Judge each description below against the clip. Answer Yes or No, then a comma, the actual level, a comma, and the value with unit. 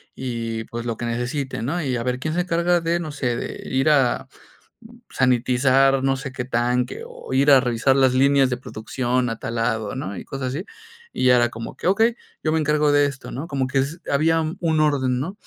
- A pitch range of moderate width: Yes, average, 3.5 semitones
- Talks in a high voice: No, low, 130 Hz